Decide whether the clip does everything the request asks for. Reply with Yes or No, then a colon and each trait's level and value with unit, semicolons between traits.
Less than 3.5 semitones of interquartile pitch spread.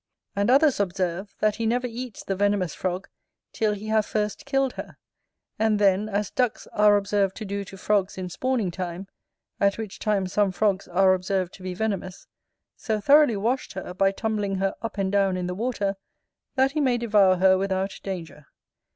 Yes: narrow, 2.5 semitones